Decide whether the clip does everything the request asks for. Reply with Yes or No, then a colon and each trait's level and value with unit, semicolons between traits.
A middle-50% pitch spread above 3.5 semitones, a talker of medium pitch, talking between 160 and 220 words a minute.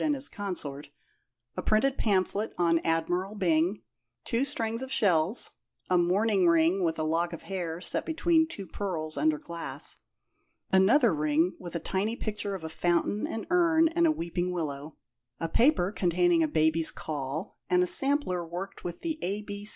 Yes: average, 5.1 semitones; medium, 180 Hz; average, 165 wpm